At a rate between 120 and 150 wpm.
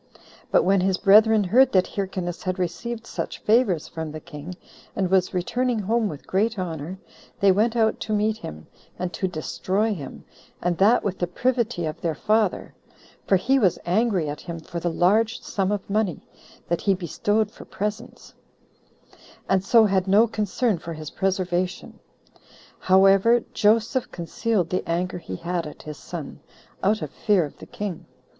No: average, 170 wpm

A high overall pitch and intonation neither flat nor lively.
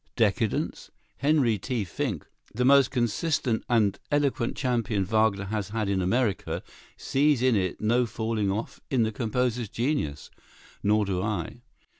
No: low, 115 Hz; average, 3.6 semitones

